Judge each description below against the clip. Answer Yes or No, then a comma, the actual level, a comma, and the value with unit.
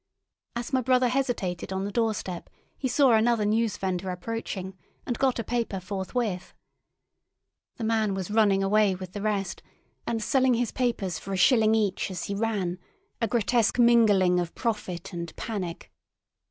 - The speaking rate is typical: Yes, average, 155 wpm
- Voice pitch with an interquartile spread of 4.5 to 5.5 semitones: No, average, 3.8 semitones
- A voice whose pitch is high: Yes, high, 215 Hz